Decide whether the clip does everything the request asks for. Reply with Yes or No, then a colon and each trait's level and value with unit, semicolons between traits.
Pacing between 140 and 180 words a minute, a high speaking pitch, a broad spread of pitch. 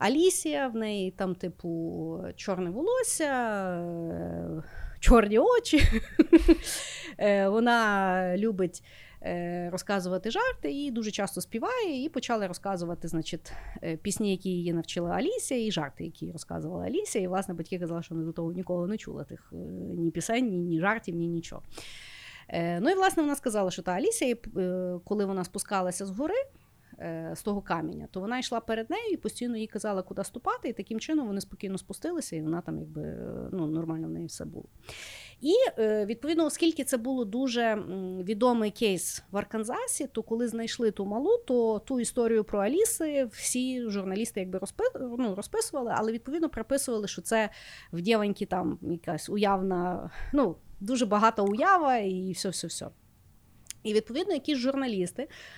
Yes: average, 150 wpm; high, 210 Hz; wide, 6.1 semitones